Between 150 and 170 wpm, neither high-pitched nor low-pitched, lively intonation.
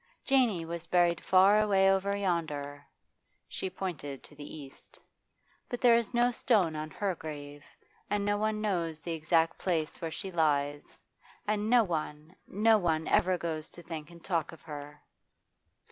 No: average, 160 wpm; medium, 170 Hz; average, 4.5 semitones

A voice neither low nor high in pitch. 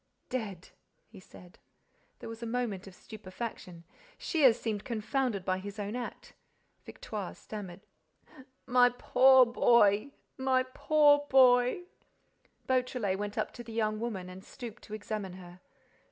No: high, 220 Hz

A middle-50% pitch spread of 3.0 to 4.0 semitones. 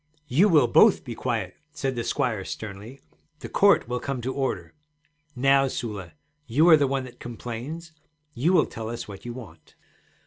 Yes: average, 3.6 semitones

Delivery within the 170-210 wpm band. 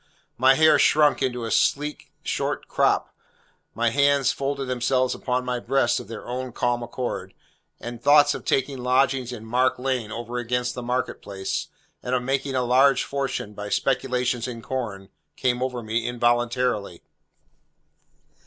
No: average, 155 wpm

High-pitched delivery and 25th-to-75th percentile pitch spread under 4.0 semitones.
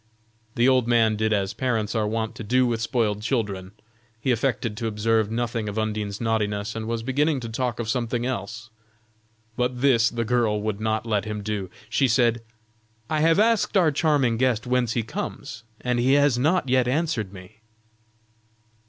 No: low, 115 Hz; average, 2.8 semitones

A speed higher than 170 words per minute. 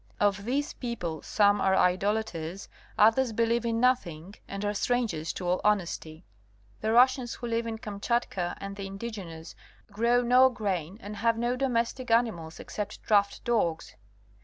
No: average, 150 wpm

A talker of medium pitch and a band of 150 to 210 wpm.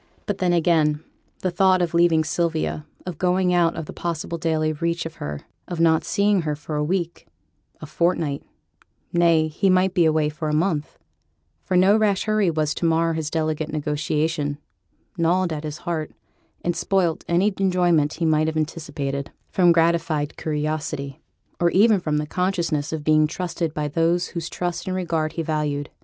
Yes: medium, 165 Hz; average, 175 wpm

